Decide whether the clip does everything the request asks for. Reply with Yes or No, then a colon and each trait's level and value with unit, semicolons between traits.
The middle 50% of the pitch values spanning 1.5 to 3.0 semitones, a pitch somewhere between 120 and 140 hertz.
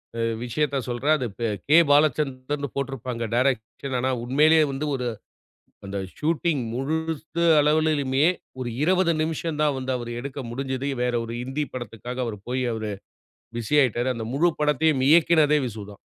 No: average, 3.7 semitones; low, 135 Hz